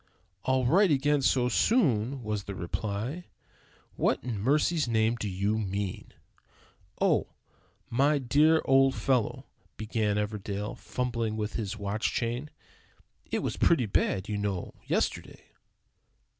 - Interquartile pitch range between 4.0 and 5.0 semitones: Yes, average, 4.5 semitones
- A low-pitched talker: Yes, low, 115 Hz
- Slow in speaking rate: Yes, slow, 125 wpm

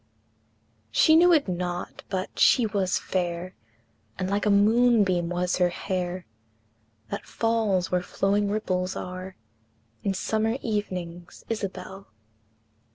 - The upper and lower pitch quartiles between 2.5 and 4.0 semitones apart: Yes, average, 2.9 semitones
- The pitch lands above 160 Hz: Yes, high, 190 Hz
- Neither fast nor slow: No, slow, 115 wpm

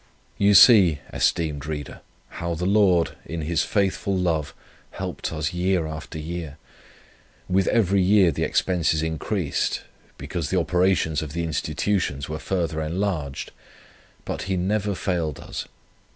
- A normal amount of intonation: Yes, average, 3.4 semitones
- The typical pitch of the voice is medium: No, very low, 85 Hz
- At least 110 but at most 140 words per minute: Yes, slow, 135 wpm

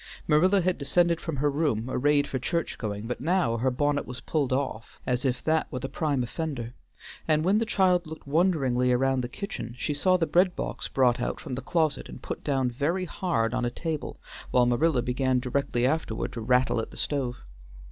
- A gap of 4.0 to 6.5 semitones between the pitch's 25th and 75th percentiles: Yes, average, 4.6 semitones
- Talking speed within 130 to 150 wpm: No, fast, 205 wpm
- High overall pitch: No, medium, 140 Hz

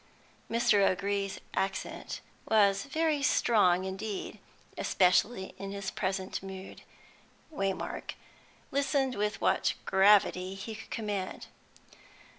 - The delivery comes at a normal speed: No, slow, 95 wpm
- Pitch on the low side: No, high, 200 Hz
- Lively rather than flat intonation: No, narrow, 2.5 semitones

